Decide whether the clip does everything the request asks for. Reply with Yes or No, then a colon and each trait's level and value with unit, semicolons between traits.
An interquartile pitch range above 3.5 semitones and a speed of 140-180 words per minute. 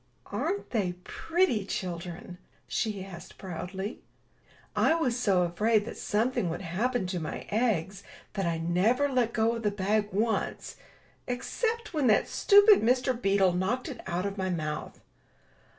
Yes: average, 5.3 semitones; average, 150 wpm